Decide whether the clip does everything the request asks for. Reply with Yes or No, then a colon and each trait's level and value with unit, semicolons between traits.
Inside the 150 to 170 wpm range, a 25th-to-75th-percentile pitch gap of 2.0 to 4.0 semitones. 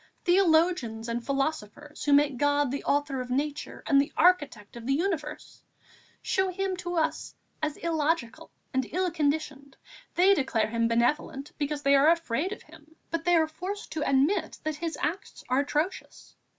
Yes: average, 165 wpm; average, 3.6 semitones